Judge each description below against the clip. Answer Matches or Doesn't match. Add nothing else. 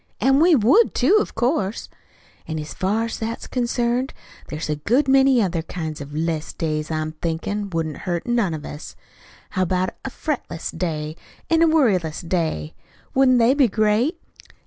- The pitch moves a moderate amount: Doesn't match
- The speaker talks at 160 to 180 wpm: Matches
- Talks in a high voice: Matches